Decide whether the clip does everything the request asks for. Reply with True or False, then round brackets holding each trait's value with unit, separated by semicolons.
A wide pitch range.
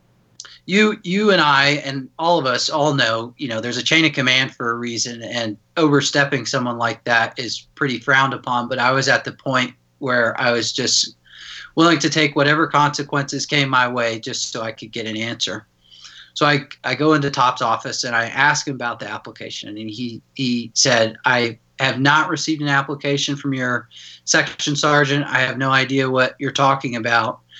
False (3.5 semitones)